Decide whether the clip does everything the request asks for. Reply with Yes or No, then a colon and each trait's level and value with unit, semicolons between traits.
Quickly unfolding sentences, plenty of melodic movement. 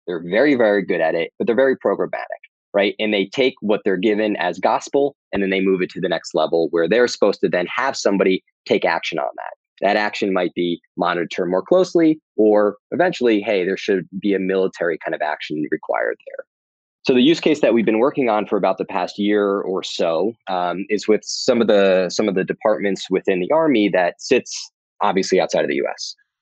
Yes: fast, 215 wpm; wide, 6.9 semitones